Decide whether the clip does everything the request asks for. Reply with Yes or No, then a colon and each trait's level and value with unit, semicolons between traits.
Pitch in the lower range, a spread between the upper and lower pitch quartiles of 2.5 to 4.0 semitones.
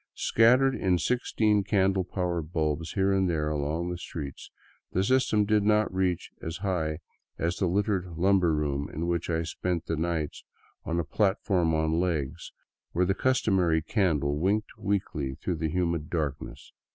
Yes: very low, 85 Hz; average, 3.5 semitones